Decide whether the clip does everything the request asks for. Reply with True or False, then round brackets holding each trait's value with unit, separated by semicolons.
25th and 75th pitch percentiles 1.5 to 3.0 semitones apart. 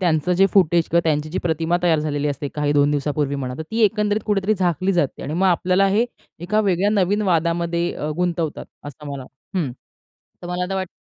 False (3.9 semitones)